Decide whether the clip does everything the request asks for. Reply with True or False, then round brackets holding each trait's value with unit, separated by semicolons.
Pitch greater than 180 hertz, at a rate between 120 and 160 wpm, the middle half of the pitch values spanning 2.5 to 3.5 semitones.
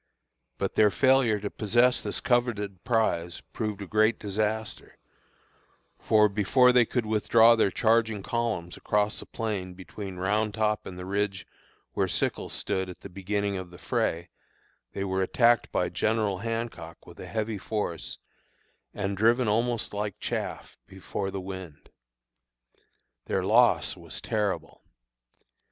False (105 Hz; 140 wpm; 2.9 semitones)